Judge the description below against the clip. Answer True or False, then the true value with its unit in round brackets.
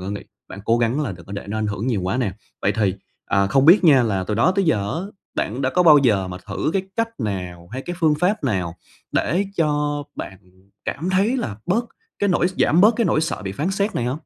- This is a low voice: True (130 Hz)